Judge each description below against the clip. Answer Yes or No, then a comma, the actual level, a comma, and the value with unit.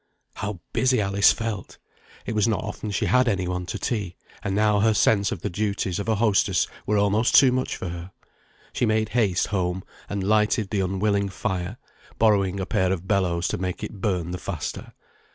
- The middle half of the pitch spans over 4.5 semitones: No, narrow, 2.5 semitones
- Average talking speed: Yes, average, 195 wpm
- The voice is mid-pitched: No, low, 100 Hz